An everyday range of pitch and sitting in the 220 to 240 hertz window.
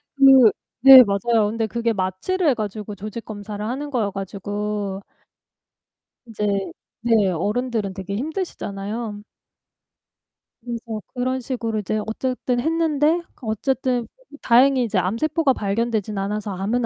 Yes: average, 3.8 semitones; high, 225 Hz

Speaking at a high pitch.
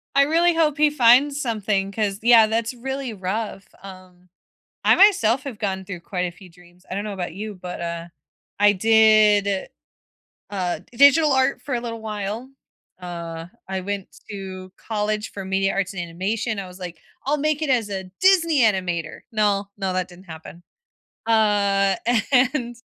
Yes: high, 205 Hz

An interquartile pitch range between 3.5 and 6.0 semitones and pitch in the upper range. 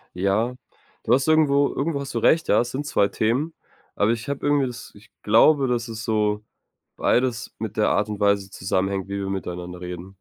No: average, 5.1 semitones; low, 110 Hz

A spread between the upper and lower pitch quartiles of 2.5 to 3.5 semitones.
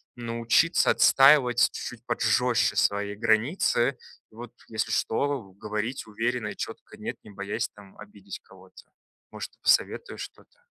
Yes: average, 2.8 semitones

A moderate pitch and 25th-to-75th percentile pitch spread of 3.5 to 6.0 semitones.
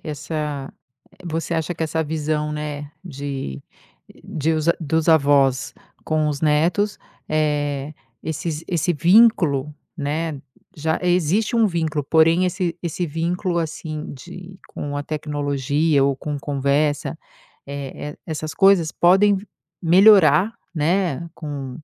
No: medium, 155 Hz; average, 2.8 semitones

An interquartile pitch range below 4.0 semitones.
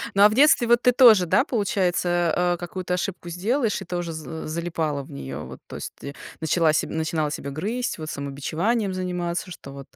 No: average, 4.3 semitones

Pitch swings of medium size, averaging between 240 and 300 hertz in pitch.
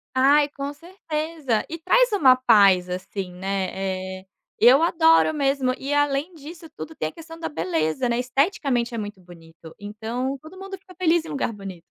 No: wide, 8.5 semitones; very high, 270 Hz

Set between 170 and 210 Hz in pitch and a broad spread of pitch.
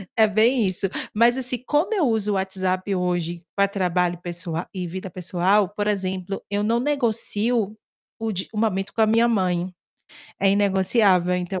No: high, 195 Hz; average, 3.3 semitones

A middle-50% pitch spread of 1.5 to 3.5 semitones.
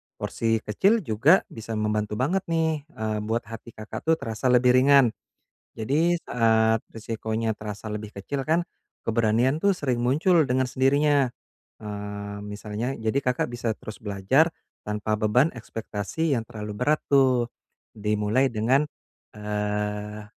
No: average, 4.1 semitones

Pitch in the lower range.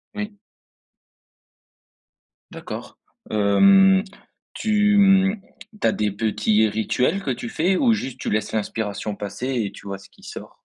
Yes: low, 120 Hz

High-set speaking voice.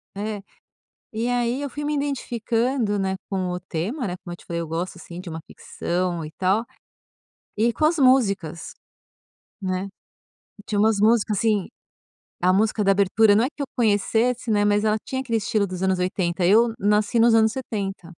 Yes: high, 210 Hz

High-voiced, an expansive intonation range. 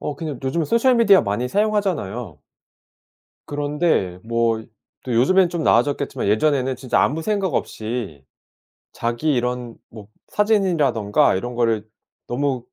No: low, 130 Hz; wide, 6.6 semitones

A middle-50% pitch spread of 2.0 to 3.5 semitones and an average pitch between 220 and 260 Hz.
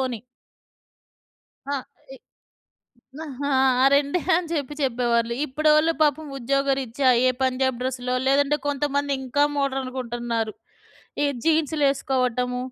No: narrow, 2.4 semitones; very high, 270 Hz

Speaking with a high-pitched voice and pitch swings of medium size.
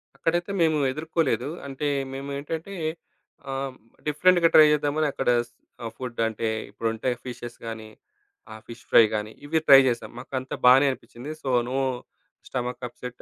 No: low, 130 Hz; average, 4.0 semitones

